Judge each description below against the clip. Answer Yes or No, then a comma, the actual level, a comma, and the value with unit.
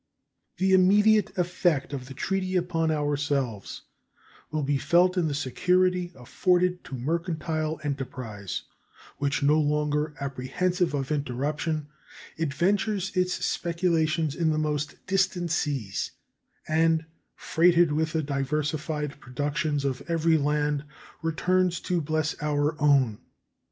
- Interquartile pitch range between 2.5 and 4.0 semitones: Yes, average, 3.4 semitones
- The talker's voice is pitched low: No, medium, 155 Hz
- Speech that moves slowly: Yes, slow, 115 wpm